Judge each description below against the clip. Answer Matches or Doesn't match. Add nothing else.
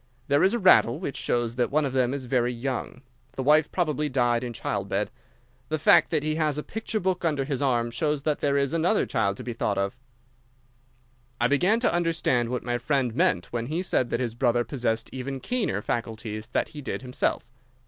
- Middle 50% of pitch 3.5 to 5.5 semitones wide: Matches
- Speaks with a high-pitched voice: Doesn't match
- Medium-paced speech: Doesn't match